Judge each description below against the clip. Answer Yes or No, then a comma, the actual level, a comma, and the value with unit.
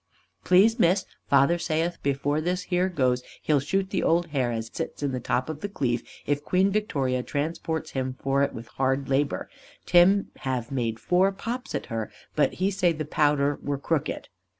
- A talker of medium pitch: Yes, medium, 145 Hz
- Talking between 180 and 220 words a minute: Yes, average, 185 wpm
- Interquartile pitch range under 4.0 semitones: No, average, 5.2 semitones